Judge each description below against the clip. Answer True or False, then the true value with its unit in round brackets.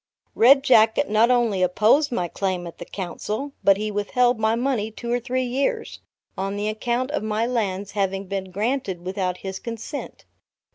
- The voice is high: True (215 Hz)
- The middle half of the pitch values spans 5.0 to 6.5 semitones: False (4.0 semitones)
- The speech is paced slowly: False (175 wpm)